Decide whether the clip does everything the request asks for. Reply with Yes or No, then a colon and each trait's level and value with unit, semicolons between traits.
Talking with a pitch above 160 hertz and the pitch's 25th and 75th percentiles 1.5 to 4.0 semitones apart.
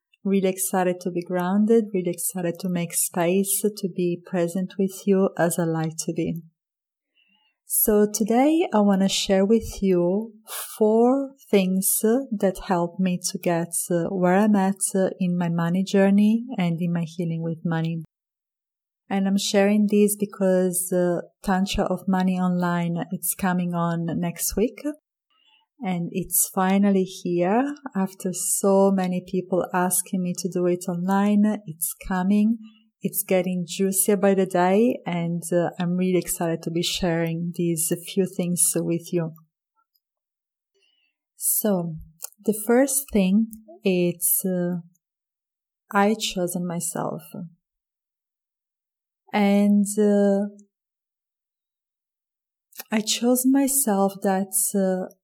Yes: high, 190 Hz; average, 2.9 semitones